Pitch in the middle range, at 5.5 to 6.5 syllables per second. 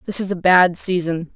No: medium, 180 Hz; 5.0 syllables/s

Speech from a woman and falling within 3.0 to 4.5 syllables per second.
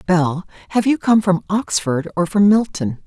Yes: female; 4.4 syllables/s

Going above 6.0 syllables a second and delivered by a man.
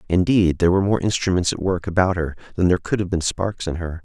Yes: 6.6 syllables/s; male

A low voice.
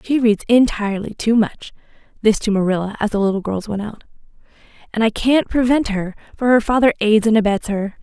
No: high, 220 Hz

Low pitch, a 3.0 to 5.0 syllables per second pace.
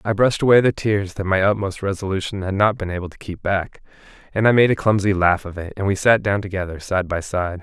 No: low, 100 Hz; 6.0 syllables/s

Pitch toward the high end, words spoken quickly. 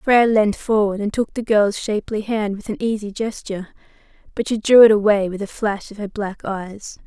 Yes: high, 210 Hz; fast, 210 wpm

